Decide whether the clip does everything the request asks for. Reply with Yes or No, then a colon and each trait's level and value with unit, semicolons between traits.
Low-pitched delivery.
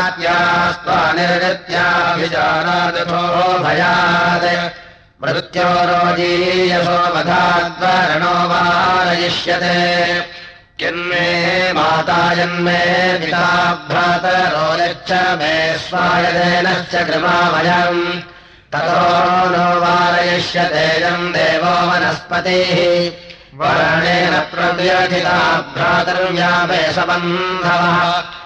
No: medium, 175 Hz